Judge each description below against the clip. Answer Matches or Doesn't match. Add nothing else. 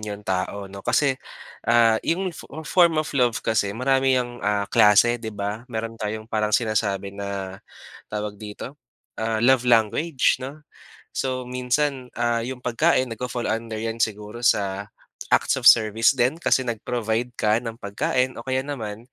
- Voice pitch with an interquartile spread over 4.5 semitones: Doesn't match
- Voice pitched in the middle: Doesn't match